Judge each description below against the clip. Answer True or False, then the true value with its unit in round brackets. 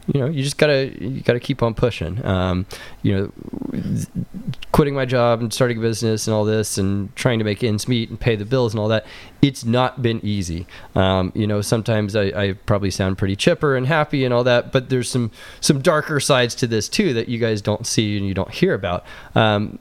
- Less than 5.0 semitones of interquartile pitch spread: True (3.7 semitones)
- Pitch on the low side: True (115 Hz)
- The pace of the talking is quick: True (225 wpm)